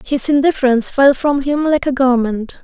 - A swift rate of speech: No, average, 180 wpm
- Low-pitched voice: No, very high, 270 Hz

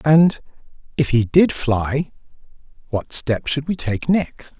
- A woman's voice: No, male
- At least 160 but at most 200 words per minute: No, average, 145 wpm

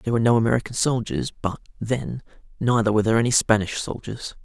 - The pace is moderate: Yes, average, 175 wpm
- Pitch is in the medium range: No, low, 115 Hz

